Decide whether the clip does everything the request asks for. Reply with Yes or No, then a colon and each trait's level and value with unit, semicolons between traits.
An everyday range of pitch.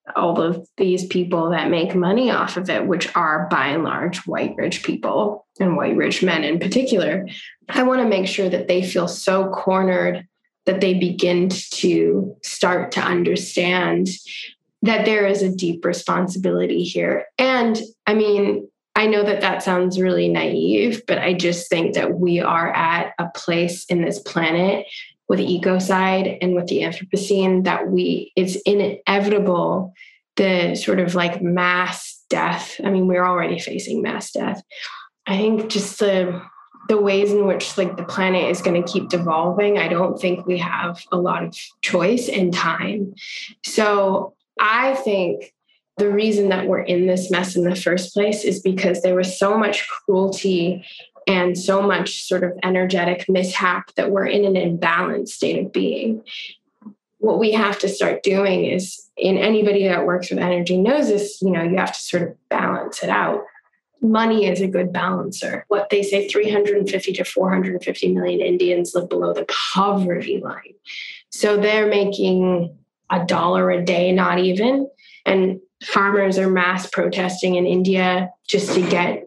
No: narrow, 2.0 semitones